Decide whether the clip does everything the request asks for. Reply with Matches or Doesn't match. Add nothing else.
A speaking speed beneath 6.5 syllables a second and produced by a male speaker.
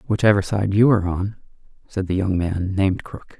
Matches